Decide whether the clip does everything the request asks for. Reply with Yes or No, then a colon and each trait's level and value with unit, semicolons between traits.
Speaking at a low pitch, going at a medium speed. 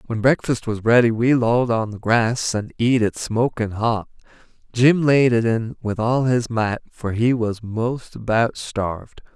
Yes: low, 115 Hz; average, 180 wpm